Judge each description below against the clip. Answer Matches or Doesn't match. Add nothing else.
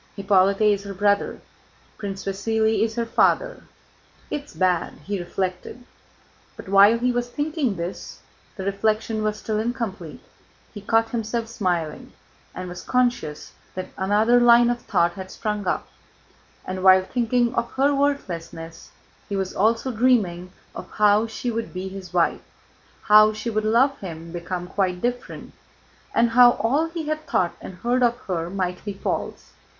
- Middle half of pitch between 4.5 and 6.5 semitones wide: Doesn't match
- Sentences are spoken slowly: Doesn't match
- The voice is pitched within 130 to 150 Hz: Doesn't match